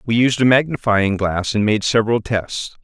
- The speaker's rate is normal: Yes, average, 190 wpm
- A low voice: Yes, low, 110 Hz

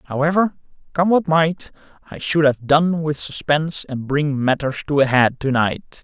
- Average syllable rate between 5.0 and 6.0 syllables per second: No, 4.5 syllables/s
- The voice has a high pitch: No, medium, 150 Hz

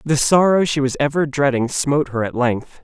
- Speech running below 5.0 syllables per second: No, 5.1 syllables/s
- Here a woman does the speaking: No, male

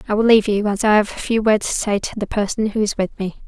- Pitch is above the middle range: Yes, high, 210 Hz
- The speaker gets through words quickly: Yes, fast, 330 wpm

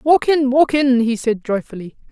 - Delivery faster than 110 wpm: Yes, average, 200 wpm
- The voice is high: Yes, very high, 255 Hz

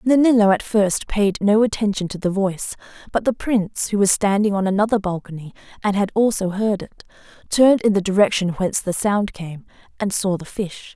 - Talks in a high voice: Yes, high, 200 Hz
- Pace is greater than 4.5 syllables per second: Yes, 5.5 syllables/s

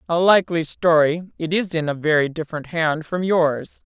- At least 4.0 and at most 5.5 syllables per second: Yes, 5.0 syllables/s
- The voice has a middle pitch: Yes, medium, 165 Hz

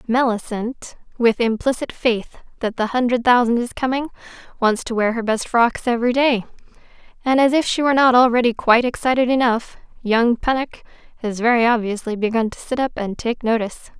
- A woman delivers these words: Yes, female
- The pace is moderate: Yes, average, 170 wpm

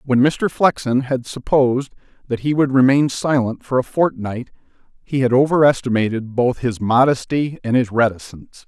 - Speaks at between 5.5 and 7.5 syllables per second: No, 5.0 syllables/s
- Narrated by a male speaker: Yes, male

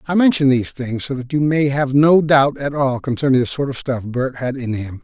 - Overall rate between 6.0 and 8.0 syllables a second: No, 5.3 syllables/s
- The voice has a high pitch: No, low, 135 Hz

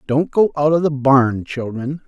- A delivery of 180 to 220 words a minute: Yes, average, 200 wpm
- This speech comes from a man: Yes, male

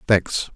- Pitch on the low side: Yes, very low, 90 Hz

